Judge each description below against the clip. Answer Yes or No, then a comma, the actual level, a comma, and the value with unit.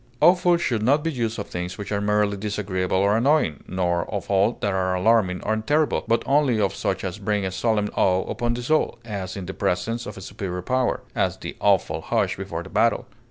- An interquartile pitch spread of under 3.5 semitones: No, average, 4.0 semitones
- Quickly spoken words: Yes, fast, 215 wpm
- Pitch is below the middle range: Yes, low, 105 Hz